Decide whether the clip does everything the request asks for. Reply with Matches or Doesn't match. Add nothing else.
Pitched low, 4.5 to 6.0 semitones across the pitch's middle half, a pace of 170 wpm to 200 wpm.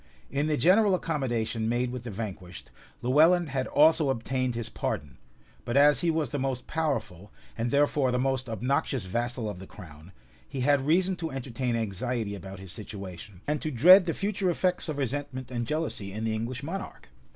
Matches